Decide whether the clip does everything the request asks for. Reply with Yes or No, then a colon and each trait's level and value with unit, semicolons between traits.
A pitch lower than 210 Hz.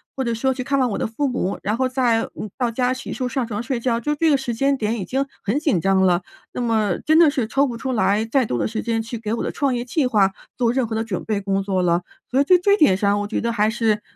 No: high, 235 Hz